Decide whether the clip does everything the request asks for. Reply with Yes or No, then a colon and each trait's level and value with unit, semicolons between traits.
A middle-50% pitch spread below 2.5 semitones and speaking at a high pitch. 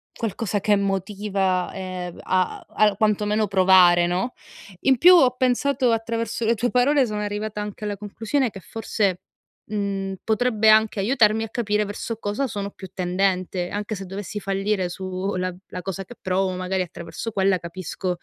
No: average, 2.8 semitones; high, 205 Hz